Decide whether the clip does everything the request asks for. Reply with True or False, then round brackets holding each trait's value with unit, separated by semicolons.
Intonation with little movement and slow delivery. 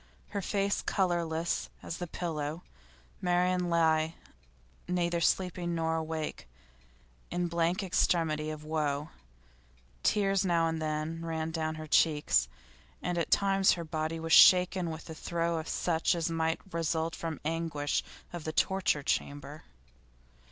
True (1.8 semitones; 130 wpm)